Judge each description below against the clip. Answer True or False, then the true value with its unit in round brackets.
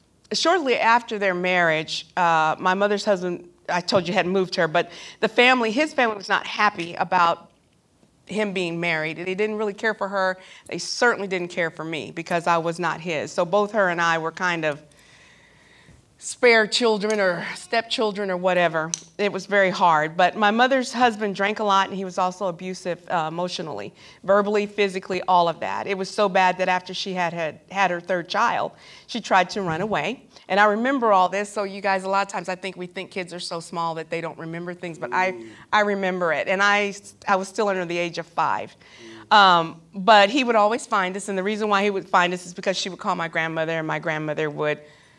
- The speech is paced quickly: True (220 wpm)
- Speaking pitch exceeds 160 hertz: True (185 Hz)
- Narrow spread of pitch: False (3.2 semitones)